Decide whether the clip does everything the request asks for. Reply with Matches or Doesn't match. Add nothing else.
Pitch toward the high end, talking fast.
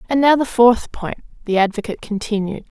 Doesn't match